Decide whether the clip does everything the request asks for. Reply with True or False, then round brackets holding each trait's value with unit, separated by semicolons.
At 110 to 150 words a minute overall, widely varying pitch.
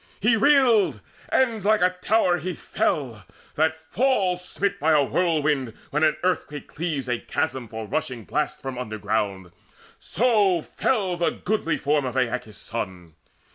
True (145 wpm; 7.0 semitones)